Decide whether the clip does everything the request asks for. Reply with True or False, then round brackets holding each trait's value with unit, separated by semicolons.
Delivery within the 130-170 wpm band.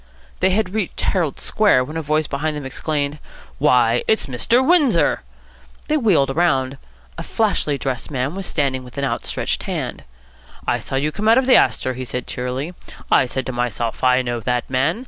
False (185 wpm)